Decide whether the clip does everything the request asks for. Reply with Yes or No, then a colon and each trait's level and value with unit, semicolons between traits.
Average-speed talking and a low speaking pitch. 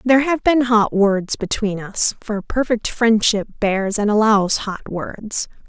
No: average, 160 wpm; high, 215 Hz